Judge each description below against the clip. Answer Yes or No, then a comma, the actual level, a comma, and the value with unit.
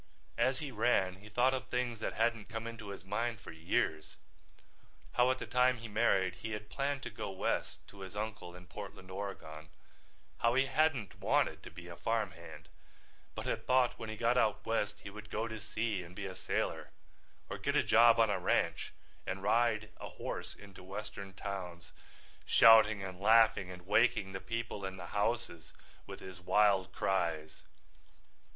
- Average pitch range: Yes, average, 3.6 semitones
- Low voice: Yes, low, 105 Hz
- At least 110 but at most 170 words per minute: No, average, 180 wpm